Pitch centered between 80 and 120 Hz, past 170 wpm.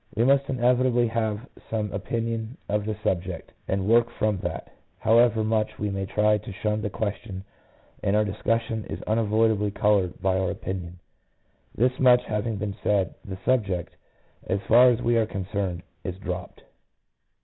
No: low, 105 Hz; average, 155 wpm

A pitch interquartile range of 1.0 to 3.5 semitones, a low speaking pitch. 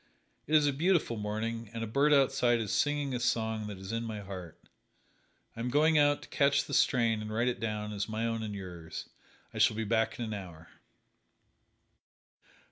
No: average, 4.3 semitones; low, 115 Hz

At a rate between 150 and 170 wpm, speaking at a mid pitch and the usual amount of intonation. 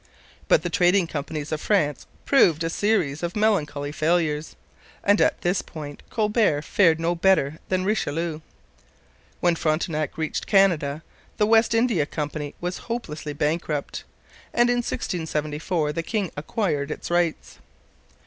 No: slow, 135 wpm; medium, 165 Hz; average, 4.4 semitones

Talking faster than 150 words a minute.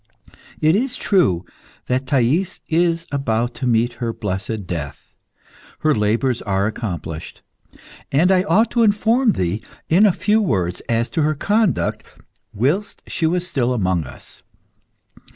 No: average, 140 wpm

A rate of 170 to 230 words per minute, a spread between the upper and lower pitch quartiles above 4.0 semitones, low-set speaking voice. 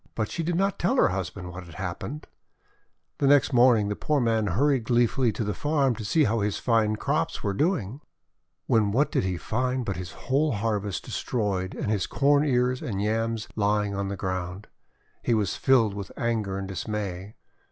Yes: average, 195 wpm; average, 4.7 semitones; low, 110 Hz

